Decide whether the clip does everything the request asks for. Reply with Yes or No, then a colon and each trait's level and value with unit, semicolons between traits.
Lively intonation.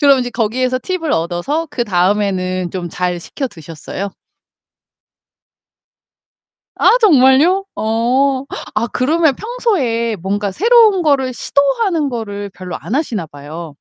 Yes: wide, 7.7 semitones